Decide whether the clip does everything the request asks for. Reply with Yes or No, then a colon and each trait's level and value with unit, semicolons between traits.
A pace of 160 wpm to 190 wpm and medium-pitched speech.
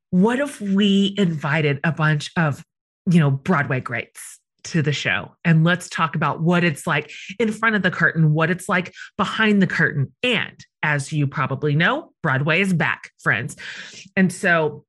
Yes: average, 175 wpm; medium, 165 Hz